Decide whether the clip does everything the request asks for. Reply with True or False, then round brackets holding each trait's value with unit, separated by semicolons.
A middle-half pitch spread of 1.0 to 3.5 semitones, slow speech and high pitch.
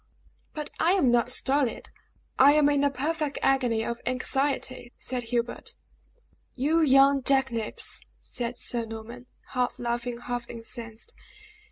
True (2.8 semitones; 130 wpm; 250 Hz)